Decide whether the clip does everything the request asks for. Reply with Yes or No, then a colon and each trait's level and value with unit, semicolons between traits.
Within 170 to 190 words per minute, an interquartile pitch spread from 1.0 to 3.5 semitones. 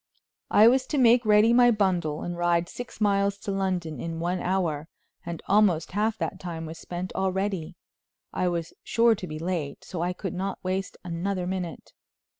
Yes: average, 180 wpm; average, 3.1 semitones